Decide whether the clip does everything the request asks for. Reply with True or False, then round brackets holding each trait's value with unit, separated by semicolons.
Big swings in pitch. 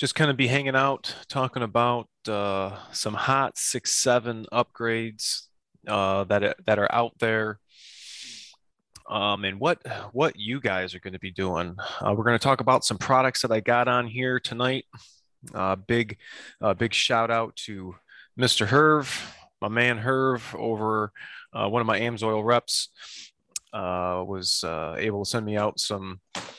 False (3.5 semitones)